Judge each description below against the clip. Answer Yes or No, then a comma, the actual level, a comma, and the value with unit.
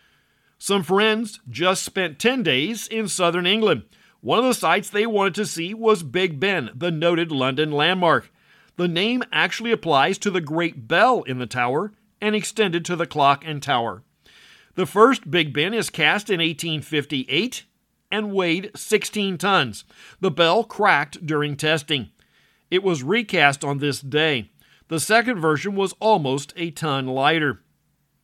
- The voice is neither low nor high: Yes, medium, 175 Hz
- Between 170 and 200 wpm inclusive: No, average, 155 wpm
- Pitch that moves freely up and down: Yes, wide, 5.7 semitones